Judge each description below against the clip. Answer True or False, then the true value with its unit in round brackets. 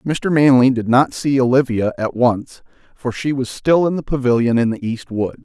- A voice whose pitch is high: False (130 Hz)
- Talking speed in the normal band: False (210 wpm)